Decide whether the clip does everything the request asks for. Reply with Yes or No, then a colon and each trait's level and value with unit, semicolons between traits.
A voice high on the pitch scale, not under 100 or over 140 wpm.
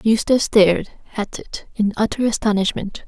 Yes: high, 210 Hz; slow, 135 wpm